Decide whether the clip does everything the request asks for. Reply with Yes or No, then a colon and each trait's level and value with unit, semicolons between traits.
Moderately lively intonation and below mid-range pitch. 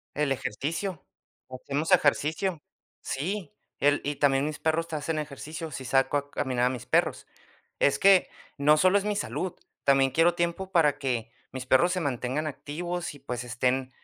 No: average, 4.2 semitones; medium, 145 Hz